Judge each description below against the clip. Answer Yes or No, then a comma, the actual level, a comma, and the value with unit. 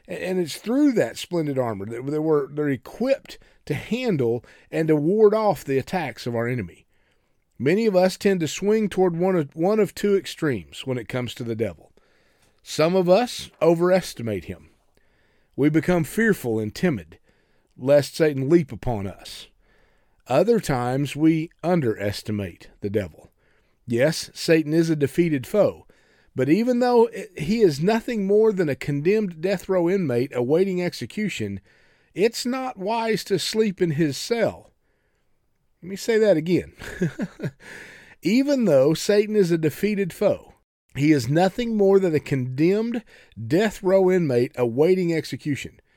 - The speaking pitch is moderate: Yes, medium, 165 Hz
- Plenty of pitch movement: Yes, wide, 7.6 semitones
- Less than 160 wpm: Yes, average, 145 wpm